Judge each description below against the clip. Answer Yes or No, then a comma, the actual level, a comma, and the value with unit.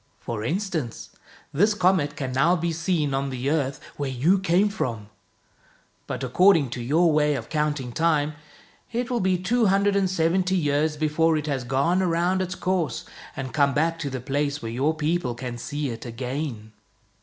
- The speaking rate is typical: Yes, average, 180 wpm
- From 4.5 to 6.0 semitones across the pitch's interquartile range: Yes, average, 5.0 semitones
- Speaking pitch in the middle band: Yes, medium, 150 Hz